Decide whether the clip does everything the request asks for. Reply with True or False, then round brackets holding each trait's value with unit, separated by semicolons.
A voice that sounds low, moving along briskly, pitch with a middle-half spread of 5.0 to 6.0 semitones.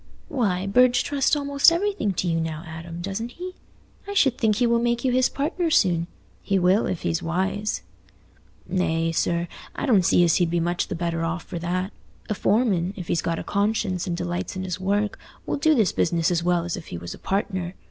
False (185 Hz; 215 wpm; 5.4 semitones)